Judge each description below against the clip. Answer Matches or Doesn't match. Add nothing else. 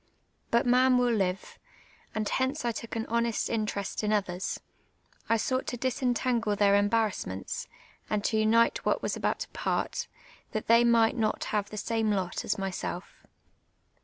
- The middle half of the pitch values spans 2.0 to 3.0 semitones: Matches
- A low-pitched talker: Doesn't match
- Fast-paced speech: Doesn't match